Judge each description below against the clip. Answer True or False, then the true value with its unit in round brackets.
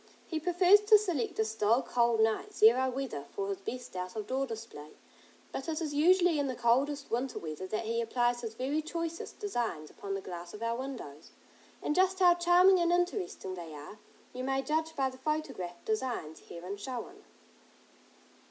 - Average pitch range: False (7.0 semitones)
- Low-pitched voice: False (255 Hz)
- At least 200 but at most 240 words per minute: False (180 wpm)